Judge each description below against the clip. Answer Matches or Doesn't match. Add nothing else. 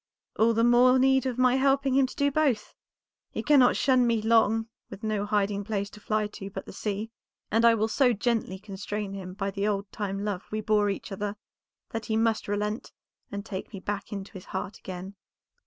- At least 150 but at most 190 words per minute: Doesn't match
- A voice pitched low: Doesn't match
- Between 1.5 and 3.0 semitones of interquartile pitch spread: Matches